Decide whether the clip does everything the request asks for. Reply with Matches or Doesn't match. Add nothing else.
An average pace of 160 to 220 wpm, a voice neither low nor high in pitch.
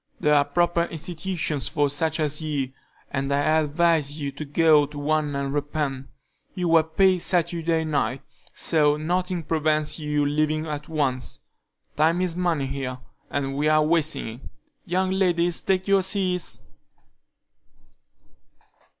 Doesn't match